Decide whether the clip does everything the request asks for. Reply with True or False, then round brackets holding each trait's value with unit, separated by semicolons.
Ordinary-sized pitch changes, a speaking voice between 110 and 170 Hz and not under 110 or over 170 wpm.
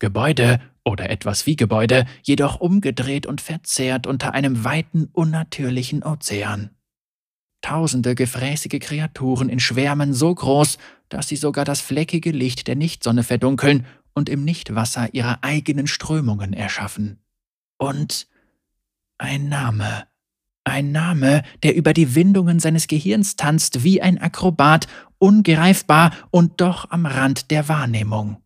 True (4.2 semitones; 140 Hz; 125 wpm)